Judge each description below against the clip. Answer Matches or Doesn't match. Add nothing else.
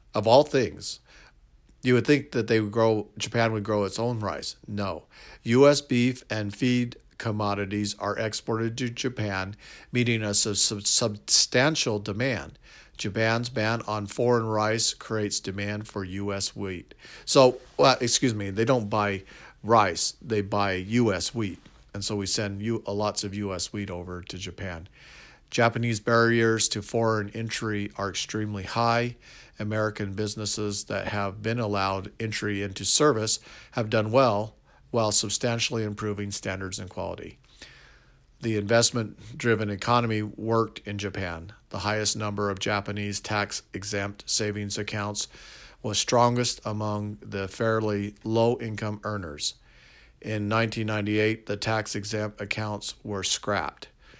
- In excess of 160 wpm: Doesn't match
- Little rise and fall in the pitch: Matches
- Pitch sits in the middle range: Doesn't match